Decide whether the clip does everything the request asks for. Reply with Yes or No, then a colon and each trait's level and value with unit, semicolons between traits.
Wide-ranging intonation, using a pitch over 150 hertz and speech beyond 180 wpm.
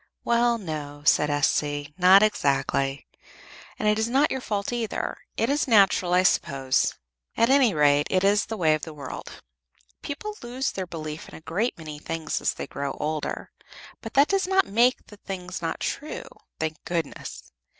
No: wide, 7.6 semitones; medium, 185 Hz; average, 175 wpm